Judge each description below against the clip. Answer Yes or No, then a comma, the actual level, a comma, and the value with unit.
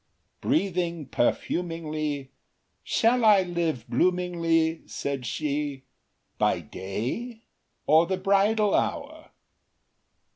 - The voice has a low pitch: No, medium, 165 Hz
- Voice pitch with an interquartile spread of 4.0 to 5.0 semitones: Yes, average, 4.7 semitones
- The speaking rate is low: Yes, slow, 80 wpm